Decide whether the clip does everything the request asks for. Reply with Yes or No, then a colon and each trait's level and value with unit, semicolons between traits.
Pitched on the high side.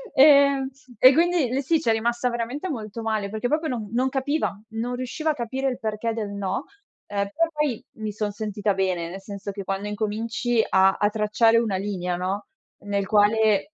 Yes: high, 220 Hz